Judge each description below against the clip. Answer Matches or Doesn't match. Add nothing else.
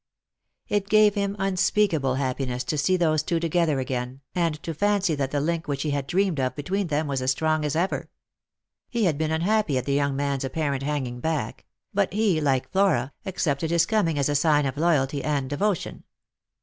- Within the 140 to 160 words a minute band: Doesn't match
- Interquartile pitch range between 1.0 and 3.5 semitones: Doesn't match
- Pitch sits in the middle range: Matches